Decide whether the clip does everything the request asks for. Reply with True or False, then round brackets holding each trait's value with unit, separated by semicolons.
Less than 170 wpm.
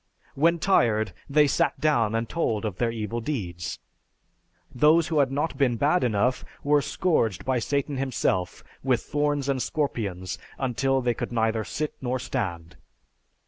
True (150 wpm)